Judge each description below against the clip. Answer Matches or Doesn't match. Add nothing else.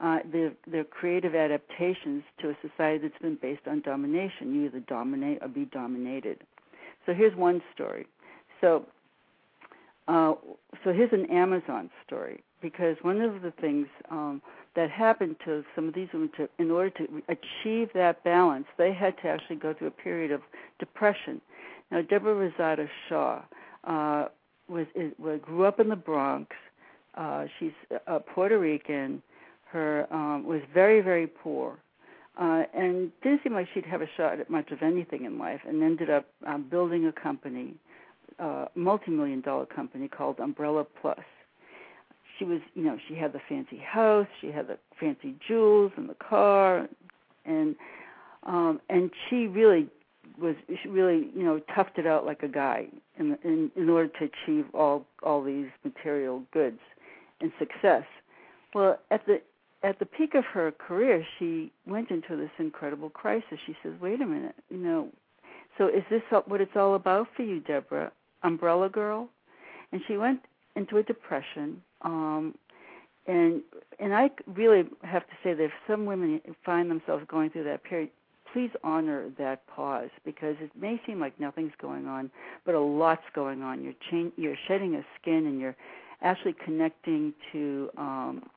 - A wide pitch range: Matches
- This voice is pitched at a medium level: Matches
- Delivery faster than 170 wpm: Doesn't match